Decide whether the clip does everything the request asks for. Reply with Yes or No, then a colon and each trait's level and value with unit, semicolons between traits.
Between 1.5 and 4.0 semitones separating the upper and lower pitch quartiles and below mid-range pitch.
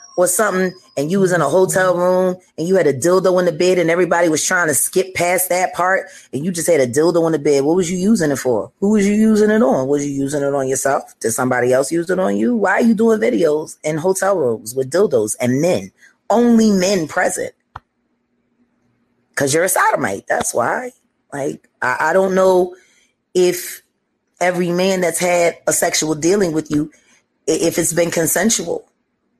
No: average, 3.6 semitones; medium, 180 Hz